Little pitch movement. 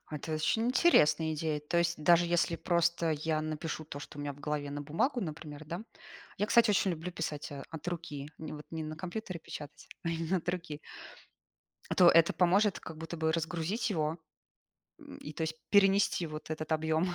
Yes: narrow, 2.2 semitones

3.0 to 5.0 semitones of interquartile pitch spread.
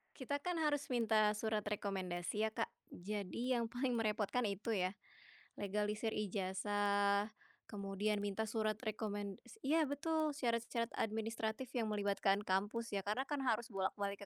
No: narrow, 2.5 semitones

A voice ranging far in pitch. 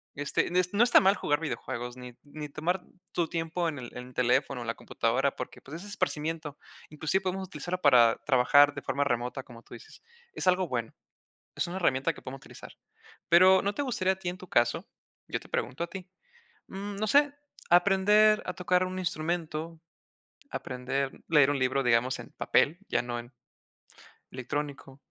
Yes: wide, 5.9 semitones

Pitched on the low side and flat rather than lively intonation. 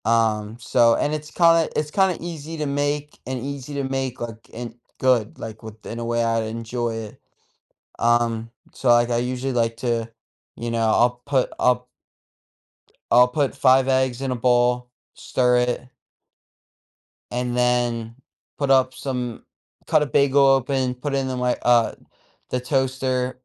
Yes: low, 125 Hz; narrow, 2.3 semitones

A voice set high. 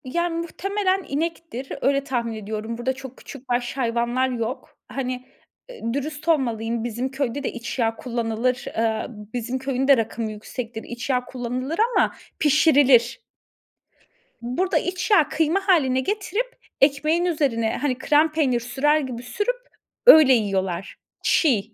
Yes: very high, 260 Hz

